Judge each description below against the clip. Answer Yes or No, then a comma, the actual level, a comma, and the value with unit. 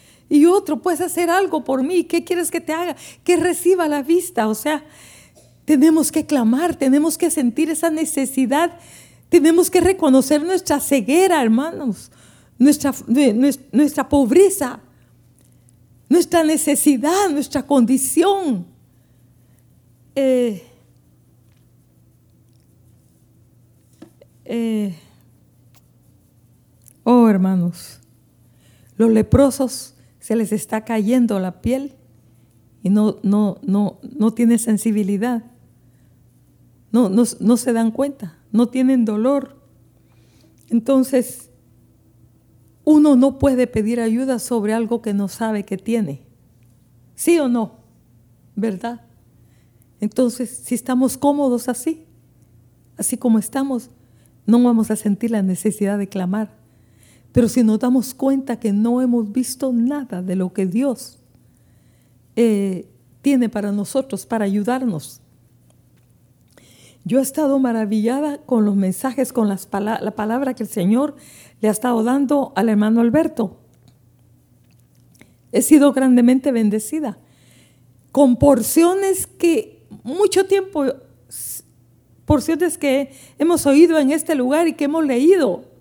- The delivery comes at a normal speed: No, slow, 115 wpm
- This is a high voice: Yes, high, 230 Hz